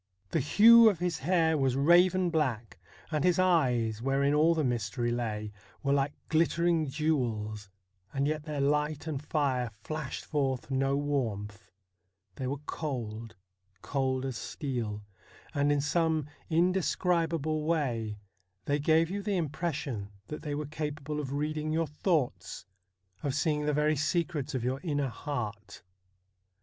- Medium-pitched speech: Yes, medium, 145 Hz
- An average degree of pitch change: Yes, average, 3.9 semitones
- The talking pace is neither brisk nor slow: Yes, average, 145 wpm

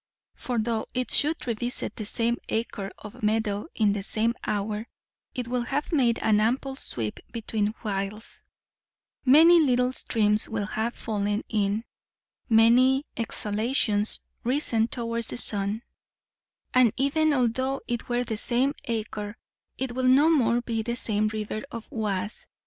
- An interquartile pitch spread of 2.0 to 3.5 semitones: Yes, average, 2.9 semitones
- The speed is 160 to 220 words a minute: No, average, 145 wpm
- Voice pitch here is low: No, high, 230 Hz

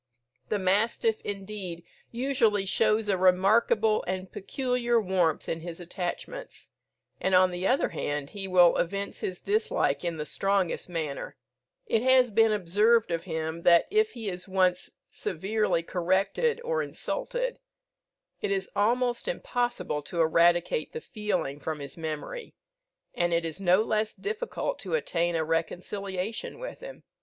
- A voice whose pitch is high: Yes, high, 195 Hz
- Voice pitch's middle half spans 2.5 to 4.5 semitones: No, average, 5.0 semitones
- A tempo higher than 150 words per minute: No, average, 145 wpm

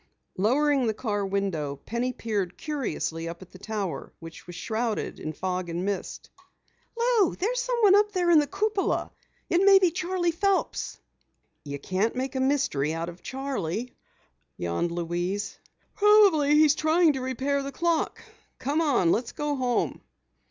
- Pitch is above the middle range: Yes, very high, 260 Hz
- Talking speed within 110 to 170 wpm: Yes, average, 155 wpm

